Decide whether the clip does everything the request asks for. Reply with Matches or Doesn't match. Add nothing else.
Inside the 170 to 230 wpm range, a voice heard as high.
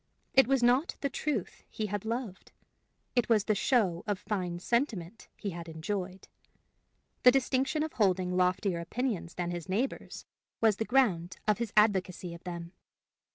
Doesn't match